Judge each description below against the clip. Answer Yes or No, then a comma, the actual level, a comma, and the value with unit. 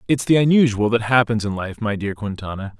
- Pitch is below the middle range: Yes, low, 115 Hz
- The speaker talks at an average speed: No, fast, 215 wpm